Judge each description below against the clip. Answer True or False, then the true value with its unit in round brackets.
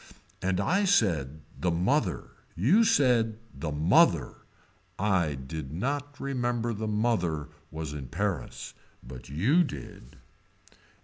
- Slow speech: True (115 wpm)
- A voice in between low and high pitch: False (95 Hz)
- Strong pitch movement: True (7.8 semitones)